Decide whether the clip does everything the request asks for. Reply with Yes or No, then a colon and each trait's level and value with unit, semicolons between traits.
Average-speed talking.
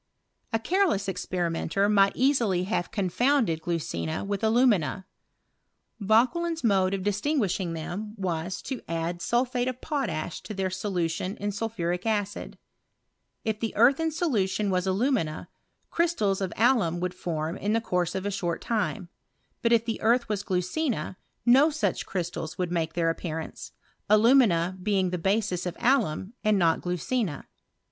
Yes: average, 145 wpm